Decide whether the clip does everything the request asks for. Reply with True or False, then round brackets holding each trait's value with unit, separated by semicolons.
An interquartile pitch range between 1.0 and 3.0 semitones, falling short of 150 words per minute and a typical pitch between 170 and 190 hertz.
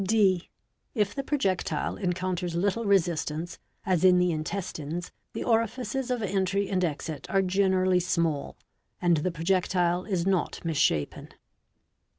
True (2.6 semitones; 140 wpm; 185 Hz)